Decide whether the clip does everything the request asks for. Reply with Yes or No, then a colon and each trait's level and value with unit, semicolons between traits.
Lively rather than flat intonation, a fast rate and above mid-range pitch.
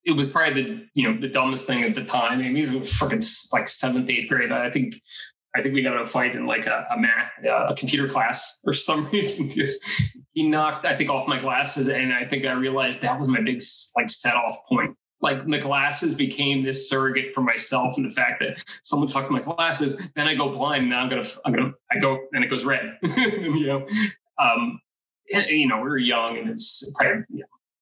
No: wide, 7.1 semitones; fast, 240 wpm; medium, 140 Hz